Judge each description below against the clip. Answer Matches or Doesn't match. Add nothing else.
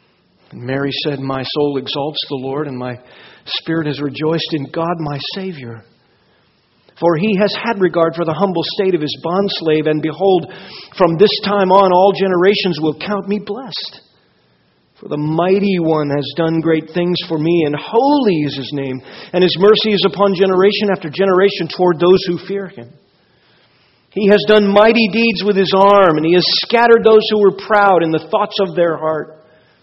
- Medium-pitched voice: Matches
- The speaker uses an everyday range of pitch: Matches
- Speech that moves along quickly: Doesn't match